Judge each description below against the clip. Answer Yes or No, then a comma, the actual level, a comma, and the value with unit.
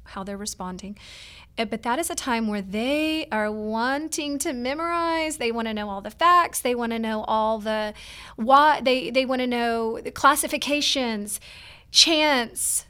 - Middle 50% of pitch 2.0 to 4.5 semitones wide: No, average, 5.1 semitones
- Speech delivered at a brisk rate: No, average, 170 wpm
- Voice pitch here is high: Yes, high, 240 Hz